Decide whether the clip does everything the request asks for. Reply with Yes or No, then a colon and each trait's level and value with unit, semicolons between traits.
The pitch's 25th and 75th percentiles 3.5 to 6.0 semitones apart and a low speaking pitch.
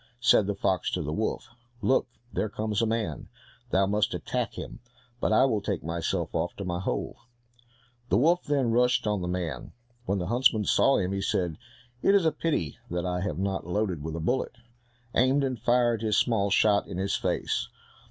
Yes: average, 4.9 semitones; low, 105 Hz